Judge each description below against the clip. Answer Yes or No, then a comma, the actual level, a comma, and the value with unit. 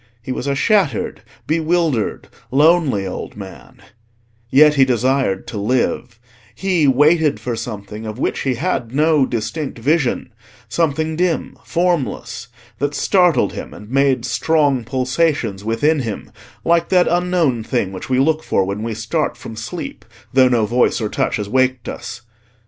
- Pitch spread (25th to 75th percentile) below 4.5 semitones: No, wide, 5.6 semitones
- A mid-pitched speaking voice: No, low, 130 Hz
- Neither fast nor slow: Yes, average, 145 wpm